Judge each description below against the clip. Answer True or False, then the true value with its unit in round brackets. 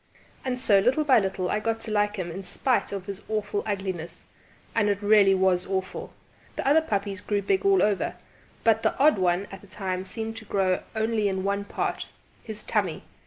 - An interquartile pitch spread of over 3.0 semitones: False (2.6 semitones)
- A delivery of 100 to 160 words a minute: False (200 wpm)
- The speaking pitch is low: False (205 Hz)